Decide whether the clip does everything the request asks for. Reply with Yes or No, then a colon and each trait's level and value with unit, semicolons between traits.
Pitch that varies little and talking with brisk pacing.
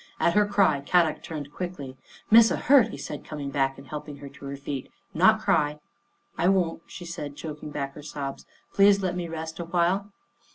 No: average, 4.4 semitones; fast, 215 wpm